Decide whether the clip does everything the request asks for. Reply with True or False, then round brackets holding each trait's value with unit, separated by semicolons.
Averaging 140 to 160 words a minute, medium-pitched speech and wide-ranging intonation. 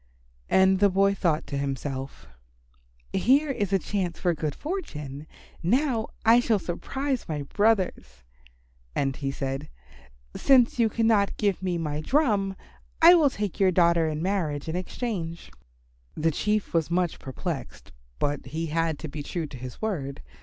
True (155 wpm; 180 Hz; 6.0 semitones)